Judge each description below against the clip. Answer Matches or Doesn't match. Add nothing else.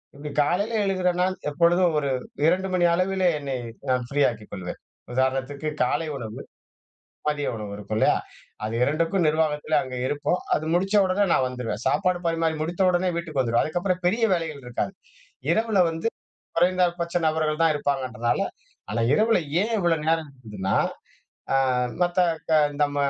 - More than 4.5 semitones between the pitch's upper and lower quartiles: Matches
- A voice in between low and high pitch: Matches